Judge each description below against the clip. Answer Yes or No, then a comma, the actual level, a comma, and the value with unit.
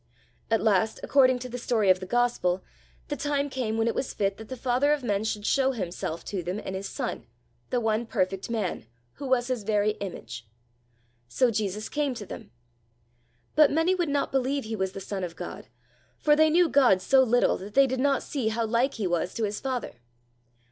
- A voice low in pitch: No, high, 230 Hz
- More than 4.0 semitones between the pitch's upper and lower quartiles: Yes, average, 5.0 semitones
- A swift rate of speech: Yes, fast, 210 wpm